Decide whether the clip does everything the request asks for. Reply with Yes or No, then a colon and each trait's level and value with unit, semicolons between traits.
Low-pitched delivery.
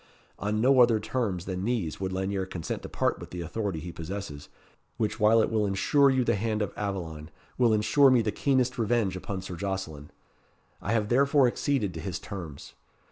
Yes: low, 100 Hz